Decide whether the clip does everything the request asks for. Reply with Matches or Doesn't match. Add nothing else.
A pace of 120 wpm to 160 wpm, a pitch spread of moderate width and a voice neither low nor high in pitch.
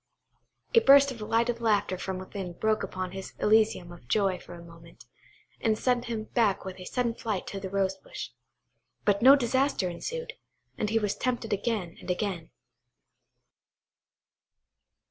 Doesn't match